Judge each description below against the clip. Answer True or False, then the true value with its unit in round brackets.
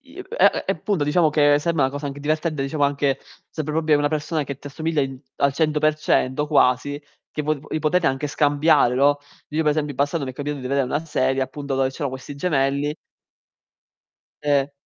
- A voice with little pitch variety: True (1.9 semitones)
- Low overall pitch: False (145 Hz)